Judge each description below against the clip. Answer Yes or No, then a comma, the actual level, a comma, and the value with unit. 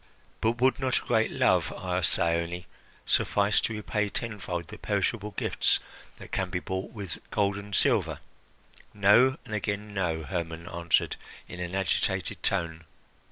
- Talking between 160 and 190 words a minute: No, average, 150 wpm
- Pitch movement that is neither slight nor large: Yes, average, 3.3 semitones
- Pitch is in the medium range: No, very low, 95 Hz